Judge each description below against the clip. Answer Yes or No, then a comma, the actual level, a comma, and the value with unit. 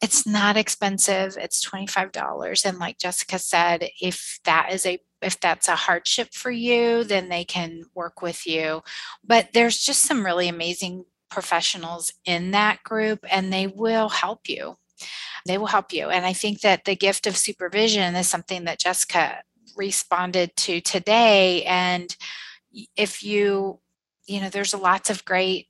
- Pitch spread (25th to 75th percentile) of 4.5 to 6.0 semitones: No, average, 2.7 semitones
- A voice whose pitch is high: Yes, high, 195 Hz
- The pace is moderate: Yes, average, 165 wpm